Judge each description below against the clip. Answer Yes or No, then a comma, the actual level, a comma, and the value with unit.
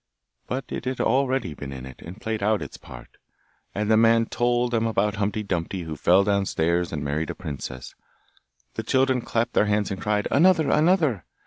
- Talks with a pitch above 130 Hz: No, low, 105 Hz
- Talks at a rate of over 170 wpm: Yes, average, 190 wpm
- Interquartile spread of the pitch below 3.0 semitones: No, wide, 5.5 semitones